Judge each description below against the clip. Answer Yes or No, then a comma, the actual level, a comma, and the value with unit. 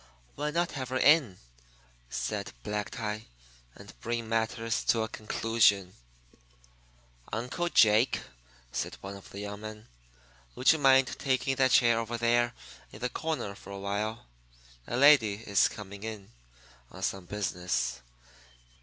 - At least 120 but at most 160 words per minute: Yes, average, 140 wpm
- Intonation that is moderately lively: Yes, average, 3.6 semitones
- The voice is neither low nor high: No, low, 115 Hz